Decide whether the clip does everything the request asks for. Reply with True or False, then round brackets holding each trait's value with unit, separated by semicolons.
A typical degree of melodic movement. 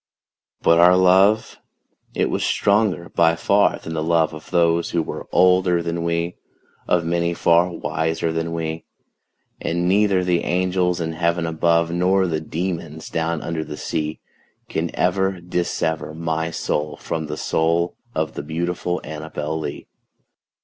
False (1.7 semitones)